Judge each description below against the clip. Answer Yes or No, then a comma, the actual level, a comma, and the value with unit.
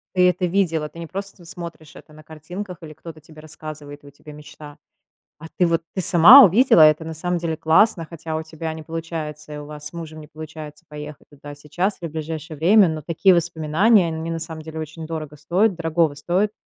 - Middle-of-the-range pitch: Yes, medium, 160 Hz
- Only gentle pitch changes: Yes, narrow, 2.1 semitones